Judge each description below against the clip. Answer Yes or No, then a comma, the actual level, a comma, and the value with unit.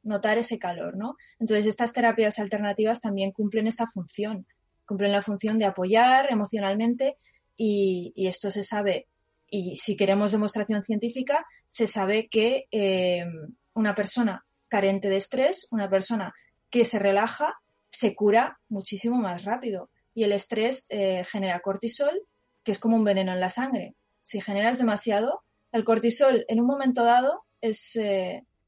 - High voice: Yes, high, 215 Hz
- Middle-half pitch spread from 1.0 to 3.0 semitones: Yes, narrow, 2.6 semitones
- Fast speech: No, average, 150 wpm